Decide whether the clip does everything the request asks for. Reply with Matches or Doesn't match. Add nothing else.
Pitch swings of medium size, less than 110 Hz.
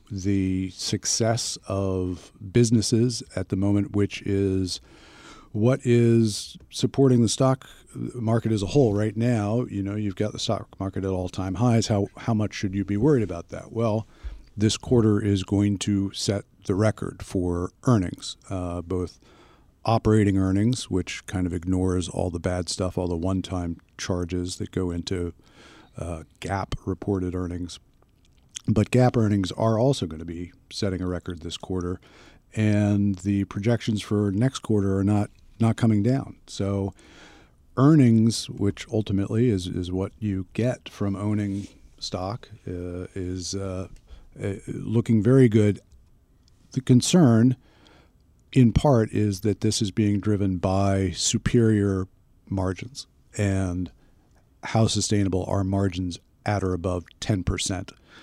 Matches